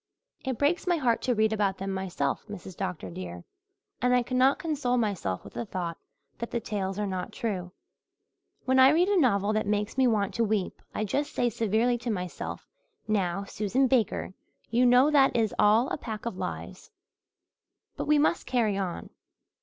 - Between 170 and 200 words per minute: Yes, average, 185 wpm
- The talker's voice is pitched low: No, high, 220 Hz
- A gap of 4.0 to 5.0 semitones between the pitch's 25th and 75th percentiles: Yes, average, 4.5 semitones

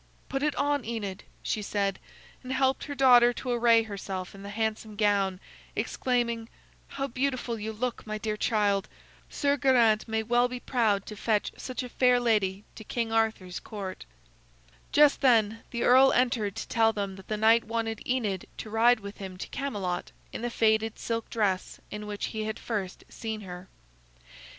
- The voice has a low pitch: No, high, 225 Hz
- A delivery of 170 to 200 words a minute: Yes, average, 175 wpm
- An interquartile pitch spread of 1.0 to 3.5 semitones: Yes, average, 2.9 semitones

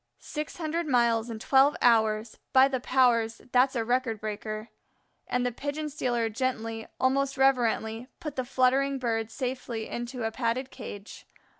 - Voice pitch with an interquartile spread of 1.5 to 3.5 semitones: Yes, average, 2.9 semitones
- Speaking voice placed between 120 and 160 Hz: No, high, 245 Hz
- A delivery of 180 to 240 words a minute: No, average, 150 wpm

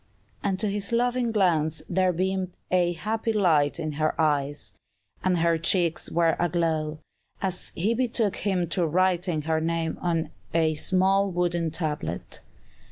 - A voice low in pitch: No, medium, 175 Hz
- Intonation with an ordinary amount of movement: Yes, average, 3.1 semitones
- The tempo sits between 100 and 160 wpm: Yes, average, 145 wpm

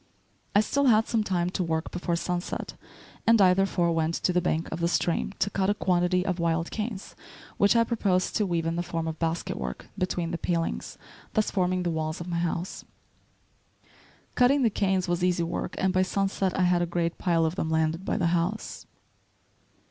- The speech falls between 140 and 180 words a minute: No, average, 200 wpm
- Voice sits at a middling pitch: Yes, medium, 180 Hz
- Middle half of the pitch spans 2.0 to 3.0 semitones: Yes, narrow, 2.5 semitones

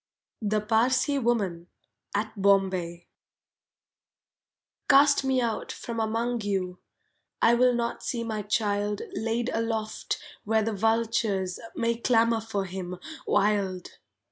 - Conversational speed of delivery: No, slow, 115 wpm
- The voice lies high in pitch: Yes, high, 220 Hz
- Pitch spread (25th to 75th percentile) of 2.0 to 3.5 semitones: Yes, average, 2.7 semitones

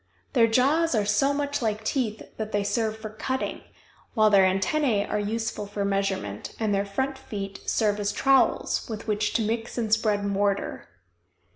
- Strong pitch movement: No, narrow, 2.6 semitones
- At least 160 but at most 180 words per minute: Yes, average, 170 wpm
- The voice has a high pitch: Yes, high, 215 Hz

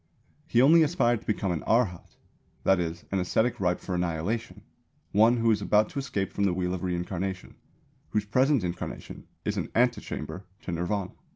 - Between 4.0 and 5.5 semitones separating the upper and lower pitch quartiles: Yes, average, 4.7 semitones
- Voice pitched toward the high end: No, low, 100 Hz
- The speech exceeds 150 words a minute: Yes, average, 175 wpm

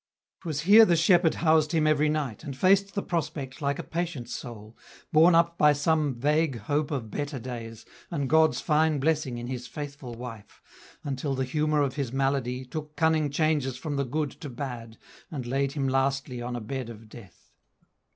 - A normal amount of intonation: Yes, average, 3.7 semitones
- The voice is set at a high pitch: No, medium, 140 Hz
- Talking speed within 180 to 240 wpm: Yes, average, 190 wpm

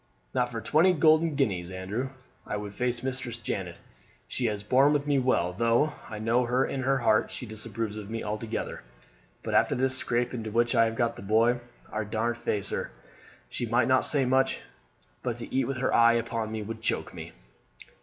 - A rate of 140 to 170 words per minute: No, average, 195 wpm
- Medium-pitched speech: No, low, 115 Hz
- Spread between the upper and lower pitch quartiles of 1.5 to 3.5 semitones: Yes, average, 3.0 semitones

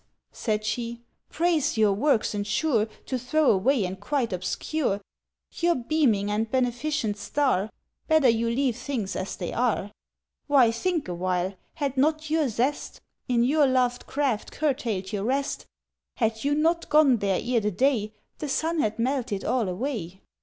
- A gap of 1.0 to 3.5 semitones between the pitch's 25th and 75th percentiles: No, average, 5.3 semitones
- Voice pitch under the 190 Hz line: No, high, 245 Hz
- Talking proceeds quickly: No, average, 155 wpm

